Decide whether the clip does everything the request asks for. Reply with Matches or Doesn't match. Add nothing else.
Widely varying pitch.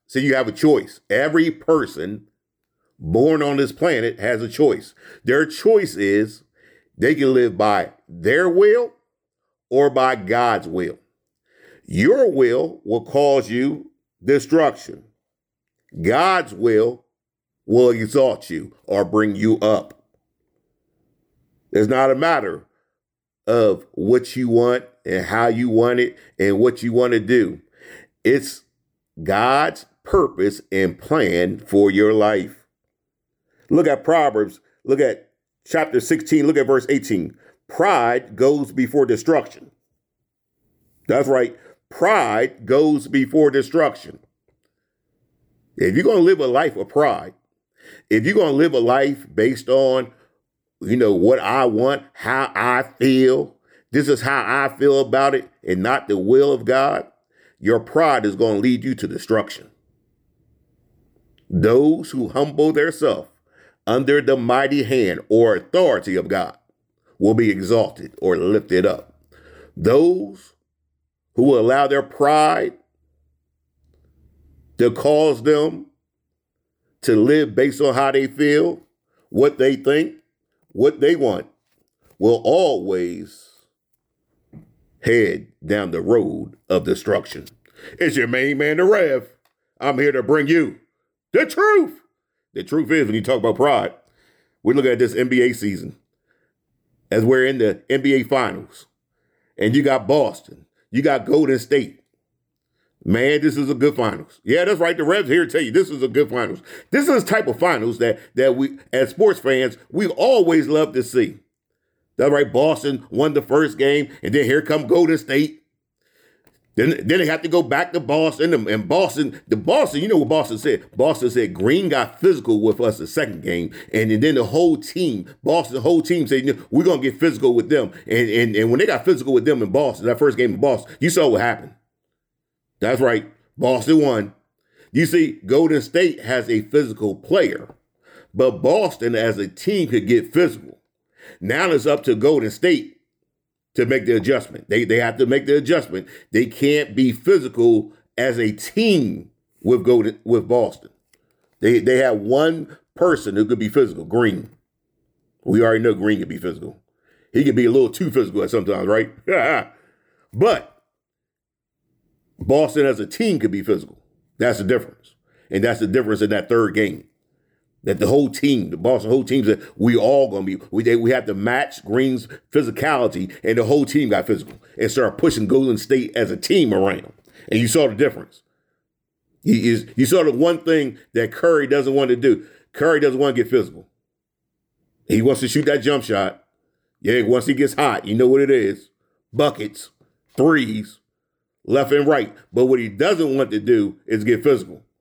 Matches